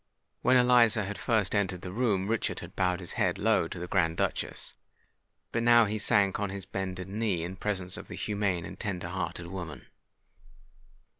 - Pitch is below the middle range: Yes, very low, 95 Hz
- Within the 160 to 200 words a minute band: Yes, average, 180 wpm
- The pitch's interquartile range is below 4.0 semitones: Yes, average, 2.9 semitones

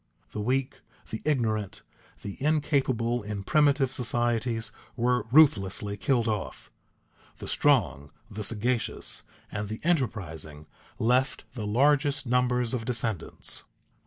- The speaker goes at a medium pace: No, slow, 110 wpm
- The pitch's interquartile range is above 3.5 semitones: Yes, average, 3.9 semitones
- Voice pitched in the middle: No, low, 120 Hz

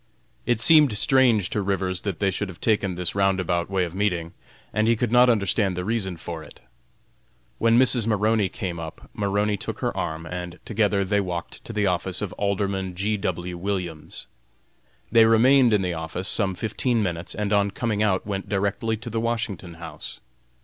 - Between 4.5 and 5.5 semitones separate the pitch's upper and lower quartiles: No, average, 3.3 semitones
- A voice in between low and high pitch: No, low, 100 Hz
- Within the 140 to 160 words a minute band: No, average, 185 wpm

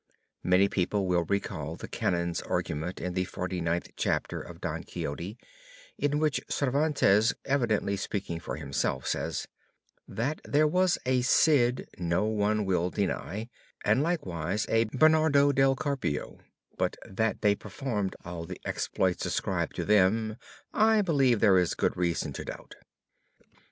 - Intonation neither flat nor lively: No, wide, 7.1 semitones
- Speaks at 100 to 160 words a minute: Yes, average, 140 wpm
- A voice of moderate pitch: No, low, 105 Hz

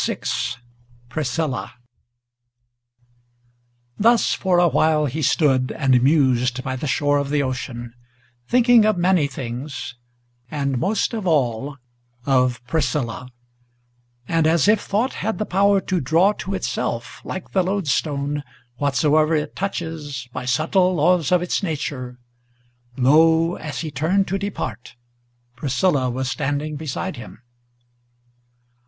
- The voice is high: No, medium, 150 Hz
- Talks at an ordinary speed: No, slow, 125 wpm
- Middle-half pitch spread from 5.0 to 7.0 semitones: Yes, wide, 5.4 semitones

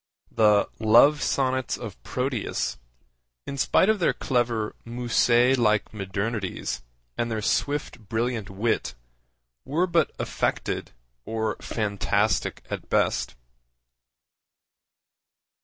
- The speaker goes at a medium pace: No, slow, 95 wpm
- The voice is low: Yes, low, 115 Hz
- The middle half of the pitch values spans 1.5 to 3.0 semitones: No, average, 3.4 semitones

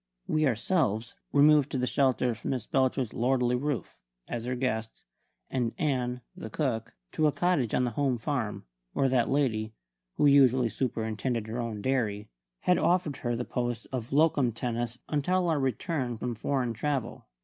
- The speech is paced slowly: No, average, 165 wpm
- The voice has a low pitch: Yes, low, 125 Hz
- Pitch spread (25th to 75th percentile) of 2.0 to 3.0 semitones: No, average, 3.4 semitones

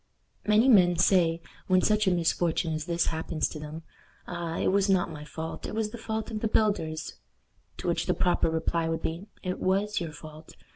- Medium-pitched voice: Yes, medium, 175 Hz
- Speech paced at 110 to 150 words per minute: No, average, 200 wpm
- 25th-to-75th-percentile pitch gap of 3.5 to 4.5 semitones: Yes, average, 3.8 semitones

